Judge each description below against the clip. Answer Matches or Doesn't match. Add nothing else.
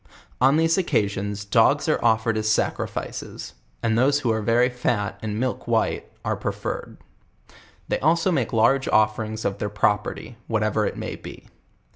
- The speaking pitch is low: Matches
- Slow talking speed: Doesn't match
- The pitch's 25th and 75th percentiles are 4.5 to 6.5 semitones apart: Doesn't match